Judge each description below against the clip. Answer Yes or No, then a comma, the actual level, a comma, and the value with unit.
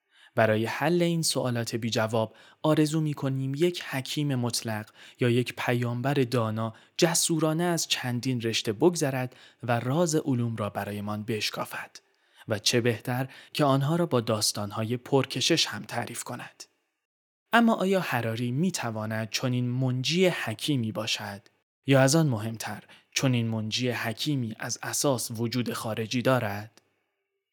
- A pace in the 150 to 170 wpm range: No, average, 135 wpm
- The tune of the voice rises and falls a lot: No, average, 4.6 semitones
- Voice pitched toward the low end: Yes, low, 125 Hz